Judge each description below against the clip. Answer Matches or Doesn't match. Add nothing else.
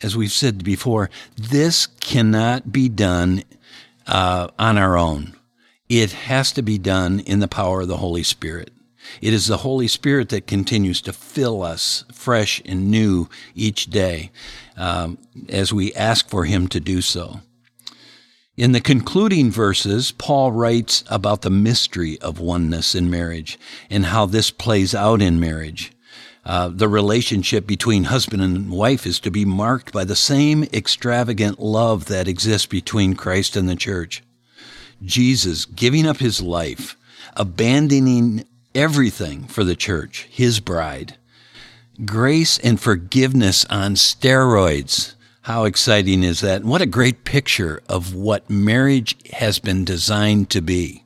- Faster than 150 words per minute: Doesn't match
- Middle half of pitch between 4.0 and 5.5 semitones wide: Matches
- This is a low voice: Matches